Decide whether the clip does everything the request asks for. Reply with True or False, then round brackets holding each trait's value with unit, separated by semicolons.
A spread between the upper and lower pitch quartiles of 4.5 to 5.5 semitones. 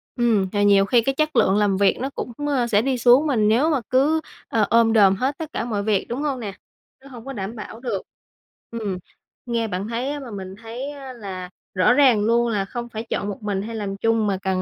False (4.0 semitones)